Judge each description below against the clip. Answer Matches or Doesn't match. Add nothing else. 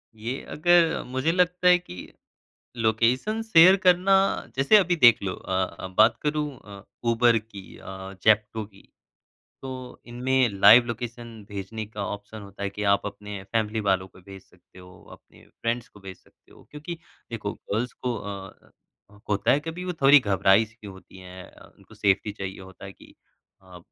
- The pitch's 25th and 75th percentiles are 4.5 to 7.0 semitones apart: Matches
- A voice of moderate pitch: Doesn't match